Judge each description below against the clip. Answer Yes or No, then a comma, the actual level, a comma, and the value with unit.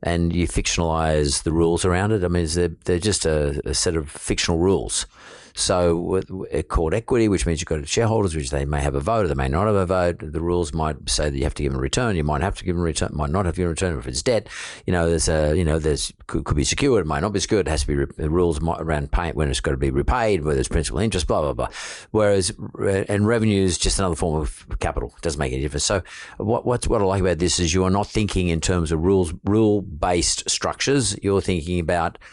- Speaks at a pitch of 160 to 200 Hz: No, very low, 85 Hz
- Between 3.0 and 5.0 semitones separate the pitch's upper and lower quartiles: Yes, average, 3.7 semitones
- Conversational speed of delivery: No, fast, 270 wpm